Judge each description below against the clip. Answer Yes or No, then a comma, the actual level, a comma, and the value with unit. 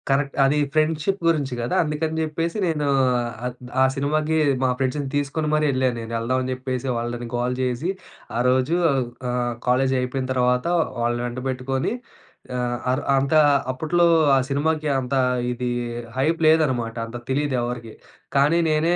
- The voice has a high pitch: No, low, 135 Hz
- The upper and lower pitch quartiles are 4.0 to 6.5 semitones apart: No, average, 3.5 semitones